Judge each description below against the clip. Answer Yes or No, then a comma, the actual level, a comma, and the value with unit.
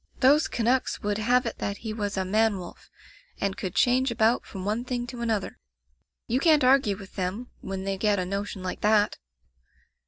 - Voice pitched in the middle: No, high, 215 Hz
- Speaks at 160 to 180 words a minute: No, average, 190 wpm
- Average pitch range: Yes, average, 3.7 semitones